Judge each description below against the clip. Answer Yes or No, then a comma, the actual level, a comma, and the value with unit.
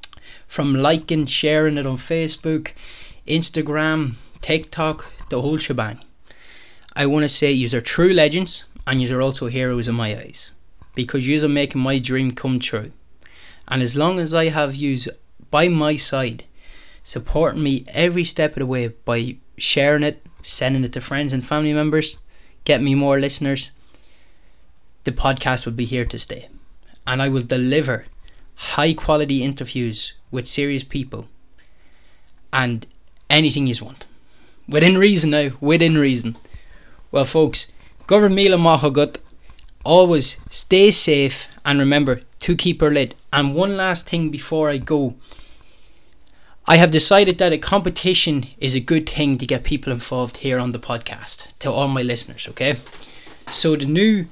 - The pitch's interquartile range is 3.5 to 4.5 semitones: Yes, average, 3.8 semitones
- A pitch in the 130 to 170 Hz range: Yes, medium, 140 Hz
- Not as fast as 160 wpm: Yes, average, 150 wpm